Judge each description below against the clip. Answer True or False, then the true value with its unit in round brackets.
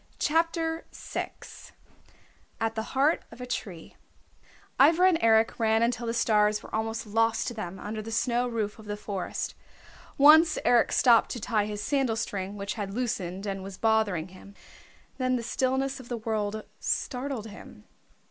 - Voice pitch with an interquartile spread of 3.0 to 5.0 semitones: True (3.3 semitones)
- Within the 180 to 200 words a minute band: False (165 wpm)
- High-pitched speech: True (225 Hz)